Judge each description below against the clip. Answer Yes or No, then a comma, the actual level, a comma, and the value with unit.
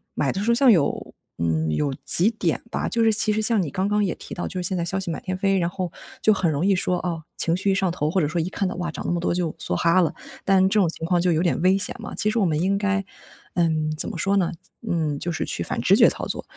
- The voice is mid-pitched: Yes, medium, 180 Hz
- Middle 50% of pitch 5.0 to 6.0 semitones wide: No, average, 2.9 semitones